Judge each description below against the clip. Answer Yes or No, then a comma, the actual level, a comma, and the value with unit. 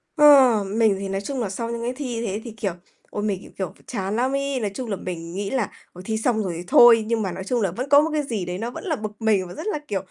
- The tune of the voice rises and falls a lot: No, average, 4.3 semitones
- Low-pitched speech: No, high, 220 Hz